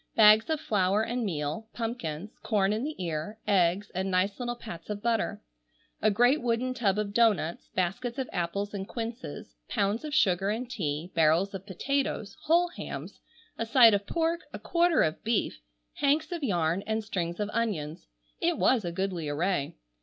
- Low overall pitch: No, high, 205 Hz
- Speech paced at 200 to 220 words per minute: No, average, 175 wpm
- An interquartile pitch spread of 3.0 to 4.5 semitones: No, average, 5.0 semitones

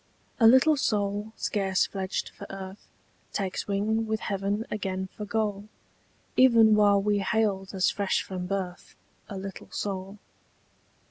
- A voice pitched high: Yes, high, 200 Hz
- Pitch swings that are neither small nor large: No, narrow, 1.9 semitones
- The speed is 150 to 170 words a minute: No, slow, 135 wpm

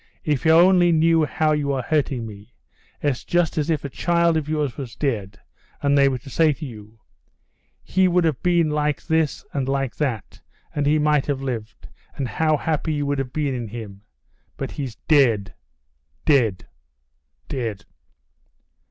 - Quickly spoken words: No, average, 170 wpm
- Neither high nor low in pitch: Yes, medium, 145 Hz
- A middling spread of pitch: Yes, average, 3.9 semitones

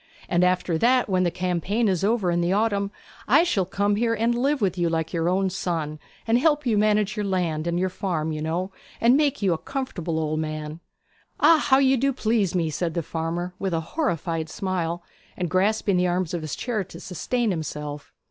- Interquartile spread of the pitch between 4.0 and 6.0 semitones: Yes, average, 4.9 semitones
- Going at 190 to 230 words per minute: Yes, fast, 205 wpm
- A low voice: No, medium, 185 Hz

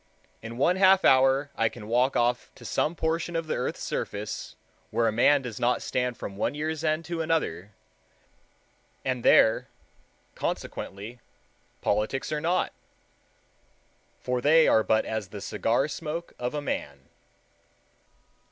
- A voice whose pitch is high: No, low, 130 Hz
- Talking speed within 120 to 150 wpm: Yes, average, 145 wpm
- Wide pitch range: Yes, wide, 5.8 semitones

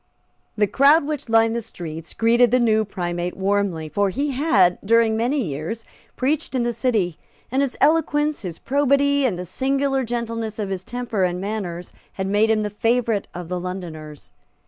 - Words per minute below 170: No, average, 175 wpm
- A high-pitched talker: Yes, high, 220 Hz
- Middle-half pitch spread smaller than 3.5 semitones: No, wide, 5.6 semitones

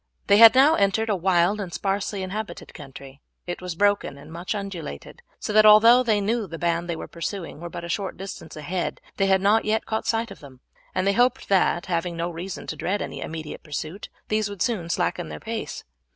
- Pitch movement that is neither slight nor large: Yes, average, 3.8 semitones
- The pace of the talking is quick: Yes, fast, 220 wpm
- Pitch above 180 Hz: Yes, high, 190 Hz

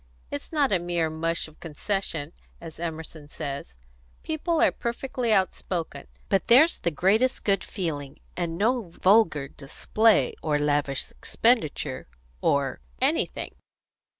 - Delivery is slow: Yes, slow, 125 wpm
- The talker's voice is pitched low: No, medium, 170 Hz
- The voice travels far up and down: Yes, wide, 6.7 semitones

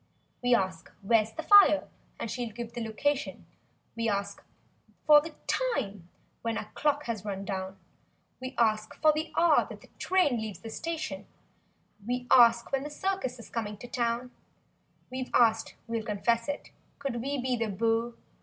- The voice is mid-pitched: No, high, 235 Hz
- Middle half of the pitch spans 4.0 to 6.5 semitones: Yes, average, 4.4 semitones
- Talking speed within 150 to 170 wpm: Yes, average, 165 wpm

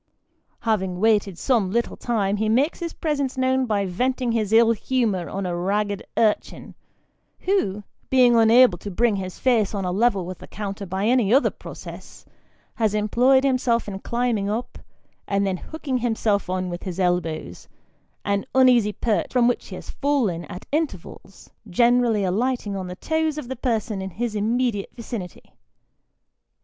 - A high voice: Yes, high, 220 Hz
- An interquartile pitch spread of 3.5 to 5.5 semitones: Yes, average, 4.2 semitones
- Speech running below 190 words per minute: Yes, average, 160 wpm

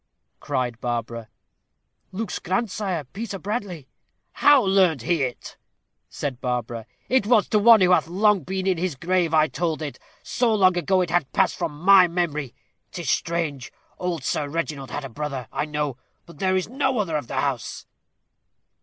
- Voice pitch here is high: No, medium, 170 Hz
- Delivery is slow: No, average, 170 wpm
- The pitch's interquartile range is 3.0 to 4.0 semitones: No, average, 5.2 semitones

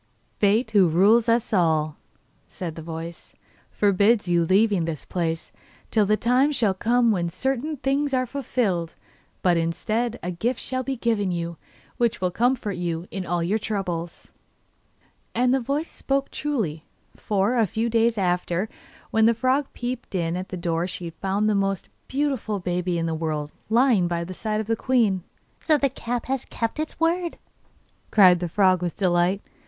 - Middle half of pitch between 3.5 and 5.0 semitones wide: No, wide, 5.6 semitones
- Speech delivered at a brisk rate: No, average, 170 wpm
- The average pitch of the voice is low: No, high, 205 Hz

